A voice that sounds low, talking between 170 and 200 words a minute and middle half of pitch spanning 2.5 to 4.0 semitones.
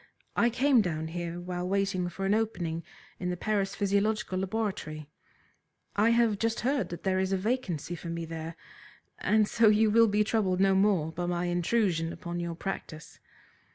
No: high, 190 Hz; average, 175 wpm; average, 3.7 semitones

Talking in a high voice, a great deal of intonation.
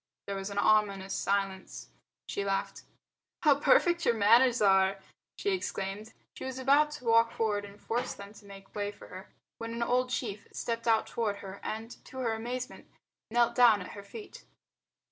No: high, 220 Hz; average, 3.5 semitones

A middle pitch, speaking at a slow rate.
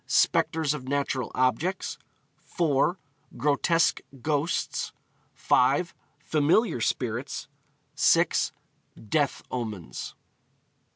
Yes: medium, 145 Hz; slow, 70 wpm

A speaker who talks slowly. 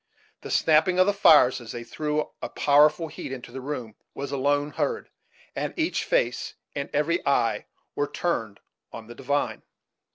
No: average, 165 wpm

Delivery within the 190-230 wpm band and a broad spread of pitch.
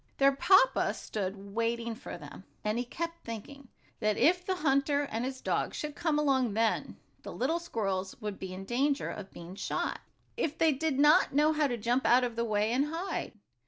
Yes: average, 195 wpm; wide, 5.7 semitones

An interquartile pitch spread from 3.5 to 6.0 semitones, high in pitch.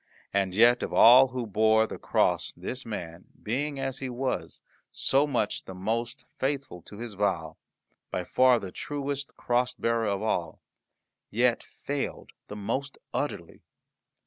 No: average, 4.3 semitones; low, 120 Hz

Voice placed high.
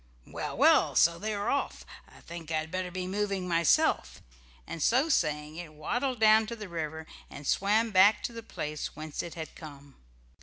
No: medium, 175 Hz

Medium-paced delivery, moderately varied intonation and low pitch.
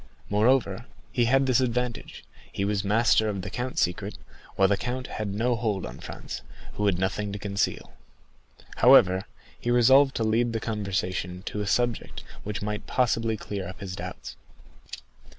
Yes: average, 165 wpm; average, 3.5 semitones; low, 105 Hz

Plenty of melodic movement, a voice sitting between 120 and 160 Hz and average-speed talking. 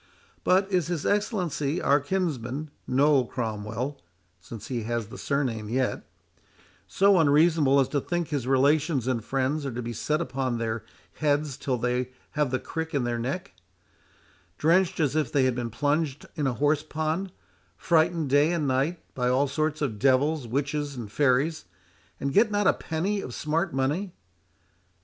No: average, 4.0 semitones; medium, 140 Hz; average, 160 wpm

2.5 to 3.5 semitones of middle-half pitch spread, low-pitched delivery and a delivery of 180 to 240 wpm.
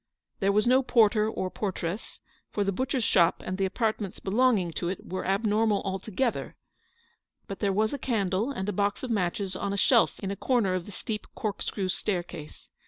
No: average, 2.8 semitones; high, 200 Hz; average, 185 wpm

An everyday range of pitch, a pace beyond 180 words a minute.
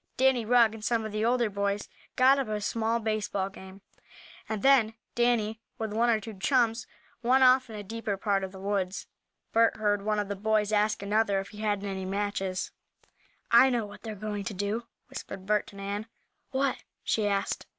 No: narrow, 2.2 semitones; average, 195 wpm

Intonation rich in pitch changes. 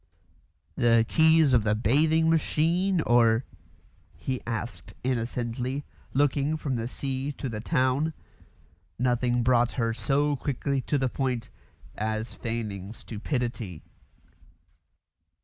No: average, 3.7 semitones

